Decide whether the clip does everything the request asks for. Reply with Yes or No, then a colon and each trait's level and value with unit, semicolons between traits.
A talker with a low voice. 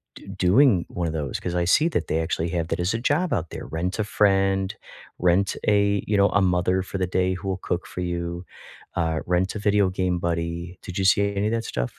Yes: very low, 95 Hz